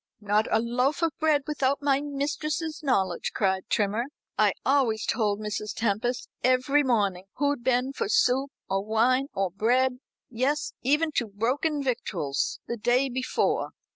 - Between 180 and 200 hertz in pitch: No, very high, 250 Hz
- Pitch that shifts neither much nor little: Yes, average, 4.7 semitones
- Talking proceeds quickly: No, average, 145 wpm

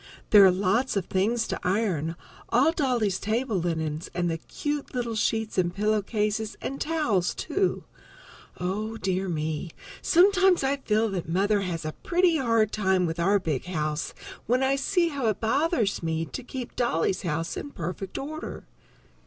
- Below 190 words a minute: Yes, average, 165 wpm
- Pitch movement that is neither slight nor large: No, wide, 6.4 semitones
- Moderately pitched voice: No, high, 210 Hz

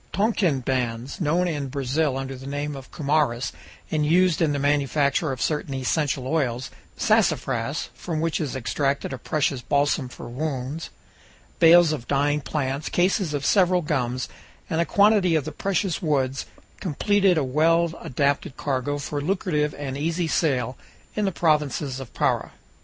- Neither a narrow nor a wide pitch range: Yes, average, 3.6 semitones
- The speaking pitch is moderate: Yes, medium, 145 Hz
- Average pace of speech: Yes, average, 150 wpm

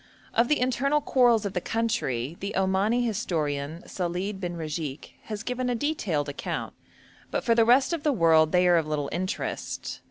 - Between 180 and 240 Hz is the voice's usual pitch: Yes, high, 190 Hz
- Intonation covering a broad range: Yes, wide, 6.6 semitones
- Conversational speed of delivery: Yes, average, 180 wpm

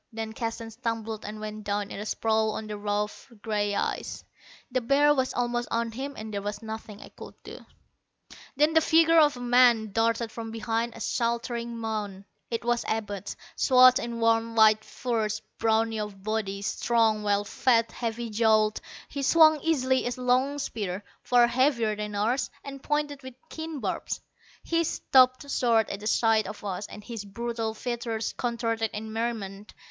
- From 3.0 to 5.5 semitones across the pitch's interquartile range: No, narrow, 2.5 semitones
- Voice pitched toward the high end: Yes, high, 230 Hz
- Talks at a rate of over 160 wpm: Yes, average, 170 wpm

